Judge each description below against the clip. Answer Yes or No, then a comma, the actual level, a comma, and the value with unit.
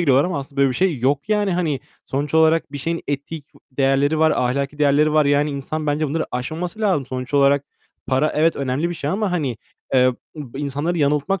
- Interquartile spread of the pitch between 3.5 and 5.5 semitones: No, narrow, 2.6 semitones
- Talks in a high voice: No, medium, 145 Hz